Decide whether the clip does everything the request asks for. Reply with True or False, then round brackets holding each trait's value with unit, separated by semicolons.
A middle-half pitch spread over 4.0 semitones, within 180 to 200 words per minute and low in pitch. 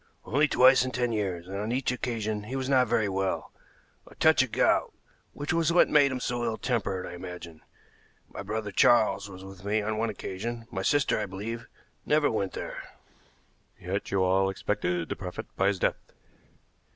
True (4.4 semitones; 190 wpm; 110 Hz)